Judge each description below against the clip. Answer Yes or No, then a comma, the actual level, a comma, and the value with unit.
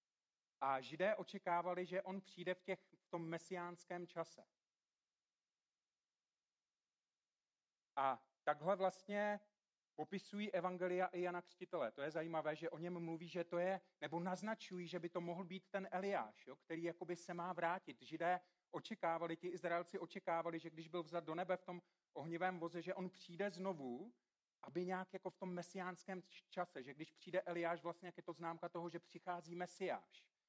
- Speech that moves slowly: No, average, 165 wpm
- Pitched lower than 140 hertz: No, medium, 175 Hz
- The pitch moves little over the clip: Yes, narrow, 1.6 semitones